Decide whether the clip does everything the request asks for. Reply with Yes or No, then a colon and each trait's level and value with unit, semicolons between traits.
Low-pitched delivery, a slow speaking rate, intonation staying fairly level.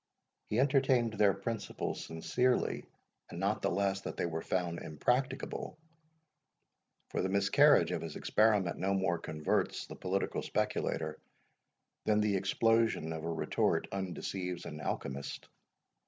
No: very low, 95 Hz; slow, 130 wpm; average, 4.3 semitones